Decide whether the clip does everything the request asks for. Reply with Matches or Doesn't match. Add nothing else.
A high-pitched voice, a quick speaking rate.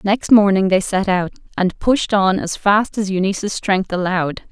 Doesn't match